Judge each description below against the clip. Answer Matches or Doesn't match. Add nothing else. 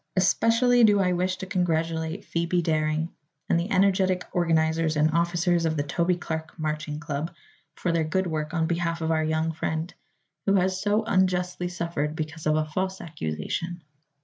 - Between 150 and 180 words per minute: Matches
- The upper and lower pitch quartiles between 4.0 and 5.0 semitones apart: Doesn't match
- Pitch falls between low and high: Matches